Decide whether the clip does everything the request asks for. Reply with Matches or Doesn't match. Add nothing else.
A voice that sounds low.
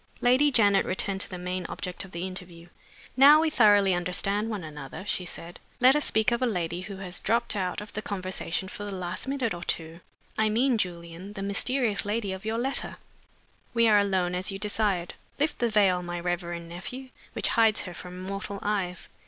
Doesn't match